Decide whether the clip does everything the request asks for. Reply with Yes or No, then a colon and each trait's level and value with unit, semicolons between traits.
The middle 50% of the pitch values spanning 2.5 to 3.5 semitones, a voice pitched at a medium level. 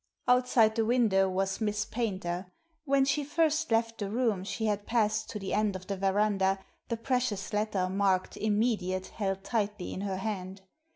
No: average, 3.0 semitones; high, 210 Hz